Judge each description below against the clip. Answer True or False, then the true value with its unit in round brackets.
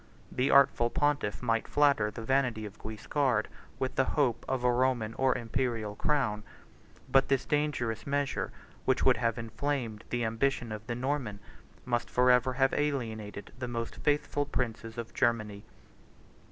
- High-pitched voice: False (120 Hz)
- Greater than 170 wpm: False (150 wpm)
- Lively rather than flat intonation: False (3.4 semitones)